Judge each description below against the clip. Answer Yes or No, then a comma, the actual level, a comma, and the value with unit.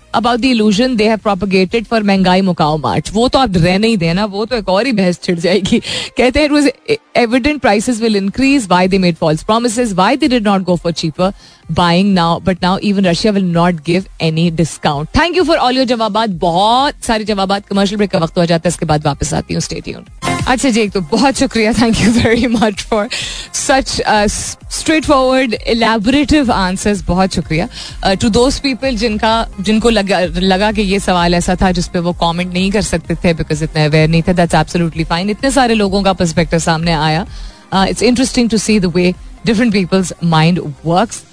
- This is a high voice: Yes, high, 200 Hz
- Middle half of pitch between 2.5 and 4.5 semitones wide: No, average, 5.0 semitones